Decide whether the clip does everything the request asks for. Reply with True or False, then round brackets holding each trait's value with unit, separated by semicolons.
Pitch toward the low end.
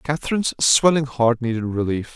True (130 Hz)